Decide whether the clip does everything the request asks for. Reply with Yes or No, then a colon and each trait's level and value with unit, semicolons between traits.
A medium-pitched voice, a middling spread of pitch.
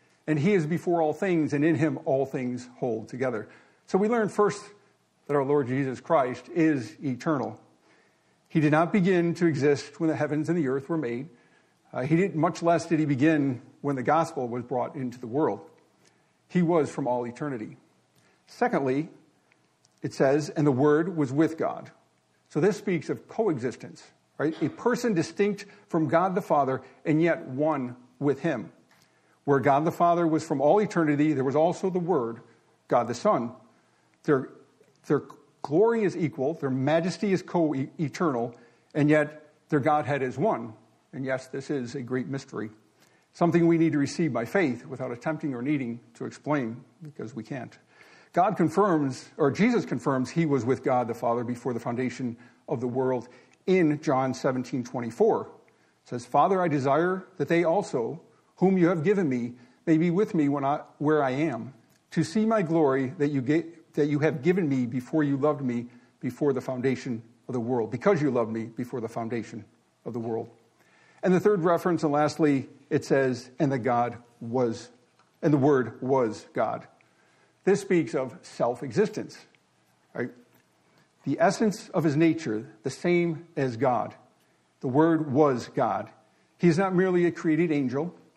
Yes: medium, 150 Hz; average, 4.6 semitones